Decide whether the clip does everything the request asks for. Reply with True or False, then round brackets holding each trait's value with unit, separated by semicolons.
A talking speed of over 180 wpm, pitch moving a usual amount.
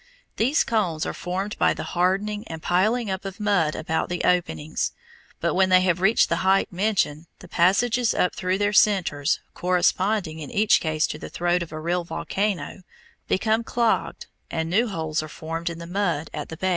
True (190 wpm; 3.9 semitones)